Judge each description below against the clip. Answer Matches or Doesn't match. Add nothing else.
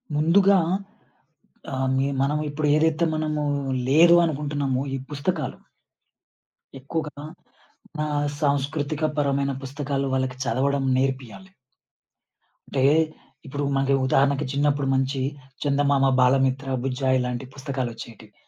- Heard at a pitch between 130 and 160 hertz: Matches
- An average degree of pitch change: Doesn't match